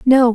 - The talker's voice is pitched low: No, high, 245 Hz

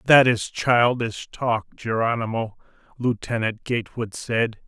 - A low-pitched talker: Yes, low, 115 Hz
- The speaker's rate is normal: No, slow, 105 wpm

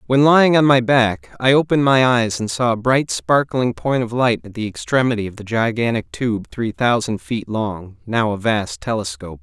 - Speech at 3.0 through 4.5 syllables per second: No, 4.9 syllables/s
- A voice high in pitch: No, low, 115 Hz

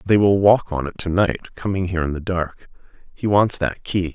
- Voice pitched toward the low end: Yes, very low, 90 Hz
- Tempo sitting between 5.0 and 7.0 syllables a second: Yes, 5.4 syllables/s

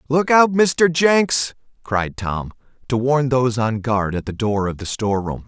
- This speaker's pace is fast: No, average, 185 wpm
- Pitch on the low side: Yes, low, 125 Hz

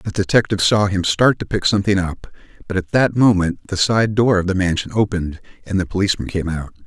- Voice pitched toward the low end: Yes, very low, 95 Hz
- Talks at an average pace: No, fast, 220 wpm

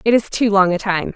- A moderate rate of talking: No, fast, 310 wpm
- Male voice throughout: No, female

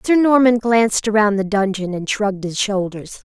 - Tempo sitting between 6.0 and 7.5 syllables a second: No, 4.8 syllables/s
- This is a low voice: No, high, 210 Hz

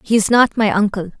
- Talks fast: Yes, fast, 250 wpm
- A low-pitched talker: No, high, 210 Hz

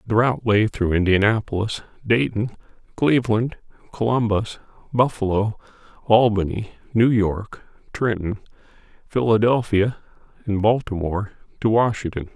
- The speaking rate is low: Yes, slow, 85 wpm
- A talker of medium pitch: No, low, 110 Hz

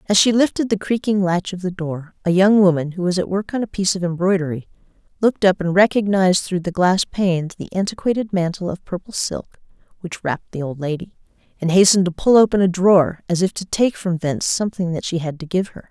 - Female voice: Yes, female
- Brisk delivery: Yes, fast, 225 wpm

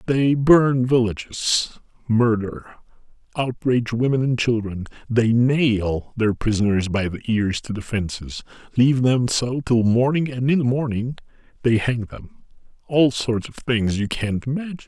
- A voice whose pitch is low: Yes, low, 120 Hz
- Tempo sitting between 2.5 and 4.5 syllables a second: Yes, 4.4 syllables/s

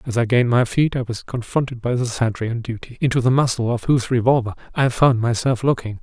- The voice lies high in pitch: No, low, 120 Hz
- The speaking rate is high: Yes, fast, 230 wpm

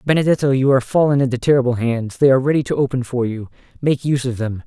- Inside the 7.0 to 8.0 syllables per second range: Yes, 7.1 syllables/s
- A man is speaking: Yes, male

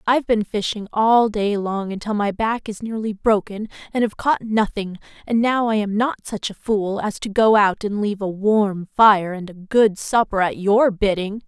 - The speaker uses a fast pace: Yes, fast, 215 wpm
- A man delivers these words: No, female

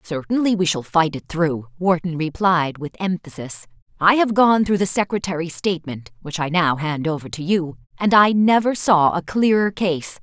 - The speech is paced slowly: No, average, 175 wpm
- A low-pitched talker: No, medium, 175 Hz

